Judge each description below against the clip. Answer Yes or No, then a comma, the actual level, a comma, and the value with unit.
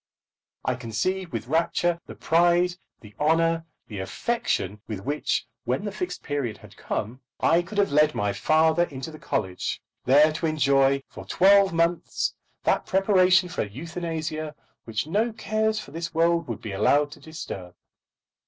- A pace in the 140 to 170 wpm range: Yes, average, 160 wpm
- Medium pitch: Yes, medium, 160 Hz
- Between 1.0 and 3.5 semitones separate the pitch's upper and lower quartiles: No, average, 4.7 semitones